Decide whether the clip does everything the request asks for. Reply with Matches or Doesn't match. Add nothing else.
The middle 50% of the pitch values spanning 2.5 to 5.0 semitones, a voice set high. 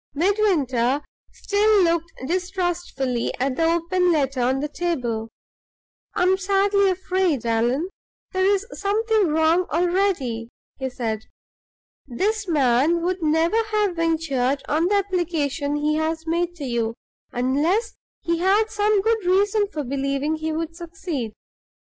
Doesn't match